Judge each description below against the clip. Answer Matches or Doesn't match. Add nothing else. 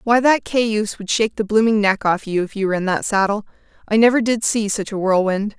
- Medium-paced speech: Doesn't match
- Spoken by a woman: Matches